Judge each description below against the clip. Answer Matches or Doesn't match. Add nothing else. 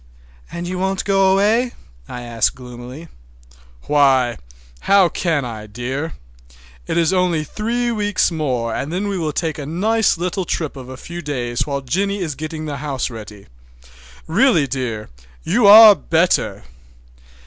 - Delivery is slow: Doesn't match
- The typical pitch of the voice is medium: Matches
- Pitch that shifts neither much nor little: Doesn't match